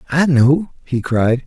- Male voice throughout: Yes, male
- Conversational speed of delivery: Yes, average, 165 wpm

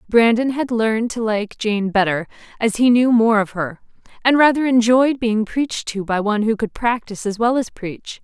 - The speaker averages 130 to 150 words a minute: No, fast, 205 wpm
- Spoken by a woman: Yes, female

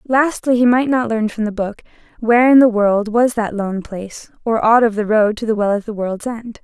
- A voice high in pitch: Yes, high, 225 Hz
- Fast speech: Yes, fast, 255 wpm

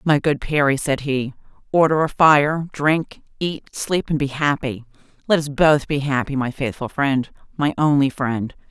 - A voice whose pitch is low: No, medium, 145 Hz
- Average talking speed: Yes, average, 170 wpm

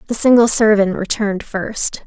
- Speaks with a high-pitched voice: Yes, high, 215 Hz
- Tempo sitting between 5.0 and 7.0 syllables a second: No, 4.8 syllables/s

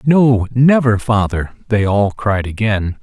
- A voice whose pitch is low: Yes, low, 110 Hz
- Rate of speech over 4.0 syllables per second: No, 3.8 syllables/s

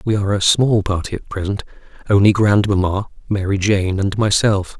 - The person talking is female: No, male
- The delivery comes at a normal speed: Yes, average, 165 wpm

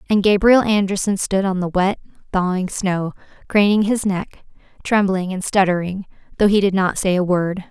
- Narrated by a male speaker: No, female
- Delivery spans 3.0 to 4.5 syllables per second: No, 4.9 syllables/s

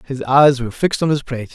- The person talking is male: Yes, male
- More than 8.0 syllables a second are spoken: No, 7.3 syllables/s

